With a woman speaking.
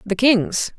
Yes: female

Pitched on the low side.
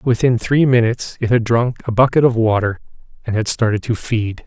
Yes: low, 115 Hz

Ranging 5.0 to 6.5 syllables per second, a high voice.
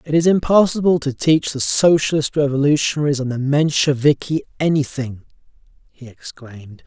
No: 5.2 syllables/s; medium, 145 Hz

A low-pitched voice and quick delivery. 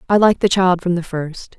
No: medium, 180 Hz; fast, 265 wpm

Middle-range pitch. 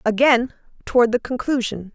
No: high, 235 Hz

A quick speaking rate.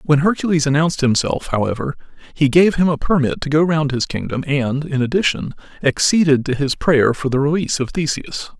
No: average, 190 wpm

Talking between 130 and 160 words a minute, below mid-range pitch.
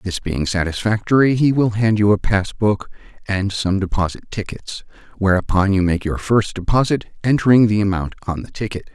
No: average, 170 wpm; low, 100 Hz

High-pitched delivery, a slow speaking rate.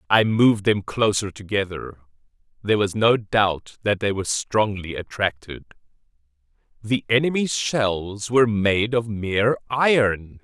No: low, 105 Hz; slow, 125 wpm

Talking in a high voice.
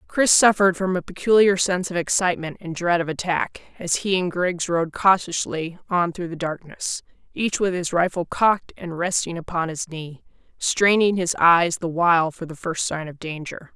No: medium, 175 Hz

